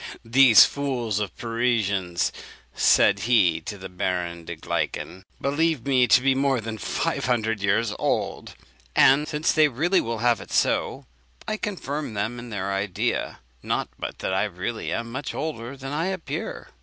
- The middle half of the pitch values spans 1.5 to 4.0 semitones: No, average, 5.2 semitones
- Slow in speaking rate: No, average, 160 wpm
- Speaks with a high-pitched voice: No, low, 115 Hz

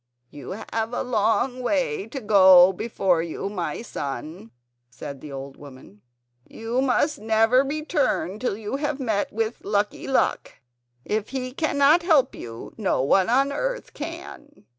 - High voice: Yes, high, 220 Hz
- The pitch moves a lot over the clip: Yes, wide, 6.8 semitones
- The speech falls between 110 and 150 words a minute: Yes, average, 140 wpm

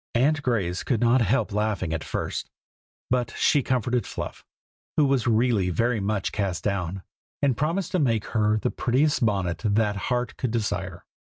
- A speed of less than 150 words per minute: No, average, 165 wpm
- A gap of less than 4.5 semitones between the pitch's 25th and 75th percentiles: Yes, average, 4.1 semitones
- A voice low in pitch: Yes, low, 115 Hz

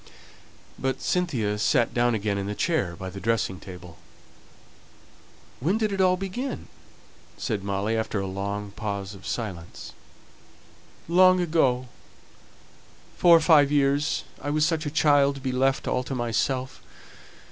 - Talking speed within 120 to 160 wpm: Yes, average, 145 wpm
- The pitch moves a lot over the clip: Yes, wide, 7.3 semitones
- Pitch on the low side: Yes, low, 125 Hz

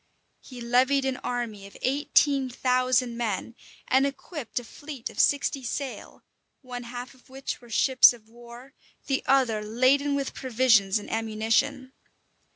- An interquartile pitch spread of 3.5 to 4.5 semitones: No, narrow, 2.4 semitones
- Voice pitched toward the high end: Yes, very high, 250 Hz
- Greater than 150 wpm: No, average, 145 wpm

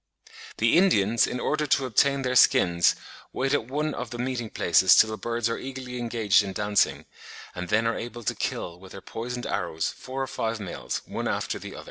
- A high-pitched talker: No, low, 115 Hz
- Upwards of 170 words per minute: Yes, fast, 205 wpm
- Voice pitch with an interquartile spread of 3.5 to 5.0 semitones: Yes, average, 3.9 semitones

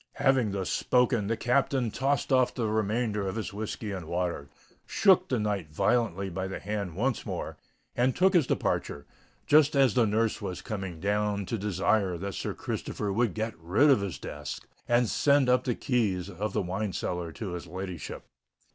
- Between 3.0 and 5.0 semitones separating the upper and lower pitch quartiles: Yes, average, 4.5 semitones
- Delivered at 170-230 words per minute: Yes, average, 180 wpm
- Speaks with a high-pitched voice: No, low, 105 Hz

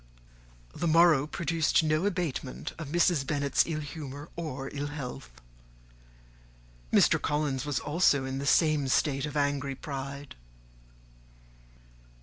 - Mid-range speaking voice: Yes, medium, 145 Hz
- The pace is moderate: No, slow, 120 wpm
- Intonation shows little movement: Yes, narrow, 2.3 semitones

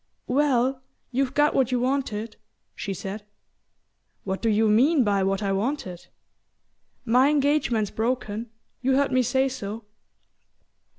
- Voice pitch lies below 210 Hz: No, high, 245 Hz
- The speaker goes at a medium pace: No, slow, 130 wpm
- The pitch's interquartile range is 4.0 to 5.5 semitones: Yes, average, 4.3 semitones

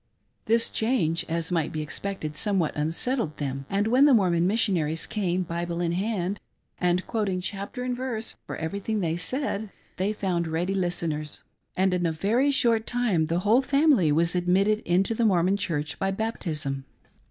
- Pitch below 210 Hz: Yes, medium, 185 Hz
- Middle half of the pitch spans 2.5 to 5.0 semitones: Yes, average, 4.7 semitones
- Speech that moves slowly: No, average, 165 wpm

